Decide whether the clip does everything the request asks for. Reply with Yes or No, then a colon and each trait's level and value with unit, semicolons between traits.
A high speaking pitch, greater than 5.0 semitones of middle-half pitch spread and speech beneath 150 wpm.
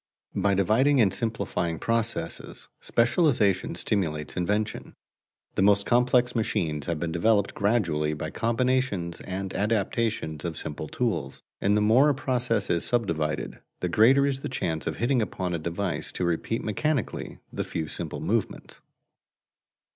No: low, 105 Hz; wide, 5.6 semitones; average, 140 wpm